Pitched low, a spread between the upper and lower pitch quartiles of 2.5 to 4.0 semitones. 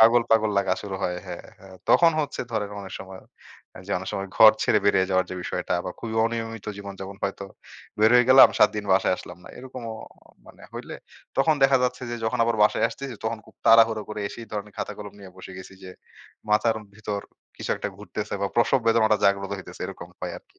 Yes: low, 105 Hz; average, 2.8 semitones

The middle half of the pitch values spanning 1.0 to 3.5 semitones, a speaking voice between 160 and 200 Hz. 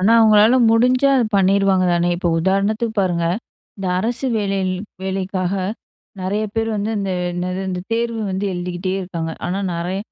Yes: average, 3.1 semitones; high, 195 Hz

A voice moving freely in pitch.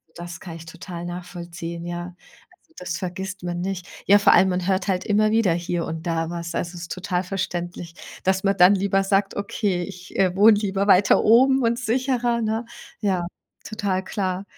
No: narrow, 2.5 semitones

